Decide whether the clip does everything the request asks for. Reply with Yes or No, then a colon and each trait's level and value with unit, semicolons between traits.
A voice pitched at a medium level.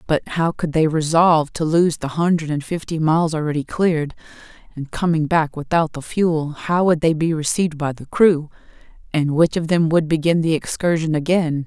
Yes: medium, 160 Hz